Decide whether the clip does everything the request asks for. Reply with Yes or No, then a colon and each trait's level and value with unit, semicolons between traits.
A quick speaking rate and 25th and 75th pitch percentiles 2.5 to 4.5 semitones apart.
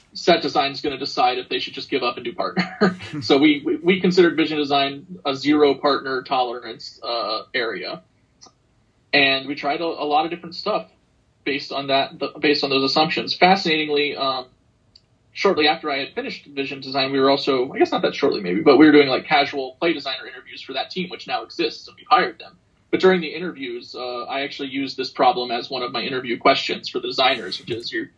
No: fast, 225 wpm; average, 4.9 semitones